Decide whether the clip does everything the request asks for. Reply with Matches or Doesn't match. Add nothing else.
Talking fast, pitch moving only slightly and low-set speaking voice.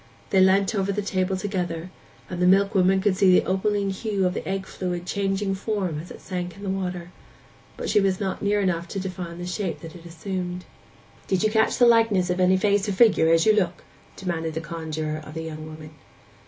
Doesn't match